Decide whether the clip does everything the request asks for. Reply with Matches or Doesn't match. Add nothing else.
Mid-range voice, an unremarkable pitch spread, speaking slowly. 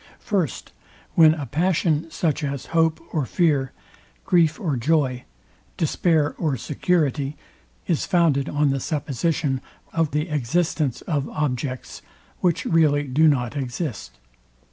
Matches